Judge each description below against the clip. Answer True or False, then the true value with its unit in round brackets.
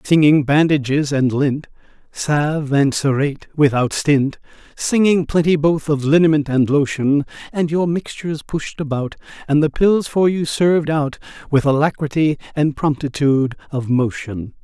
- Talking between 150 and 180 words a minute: False (140 wpm)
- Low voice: False (145 Hz)